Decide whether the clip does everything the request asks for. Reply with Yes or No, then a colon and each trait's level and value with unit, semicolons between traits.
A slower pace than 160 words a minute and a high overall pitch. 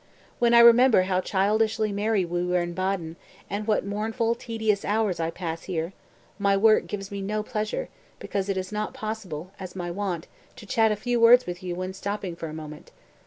No: fast, 205 wpm; high, 200 Hz